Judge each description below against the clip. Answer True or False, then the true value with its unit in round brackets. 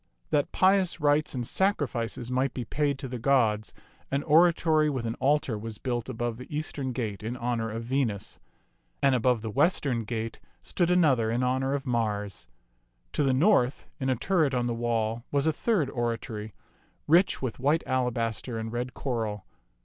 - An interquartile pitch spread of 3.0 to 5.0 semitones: True (4.0 semitones)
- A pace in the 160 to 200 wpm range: True (170 wpm)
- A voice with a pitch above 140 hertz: False (125 Hz)